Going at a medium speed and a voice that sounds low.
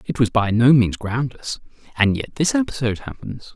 Yes: average, 170 wpm; low, 120 Hz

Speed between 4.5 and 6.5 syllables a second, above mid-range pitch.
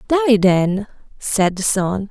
No: 3.7 syllables/s; high, 210 Hz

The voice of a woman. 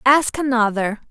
Yes: female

